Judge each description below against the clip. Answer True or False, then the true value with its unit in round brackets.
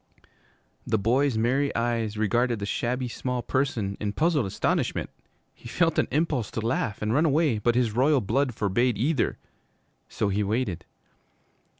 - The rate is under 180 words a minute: True (155 wpm)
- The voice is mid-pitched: False (120 Hz)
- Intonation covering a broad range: False (3.9 semitones)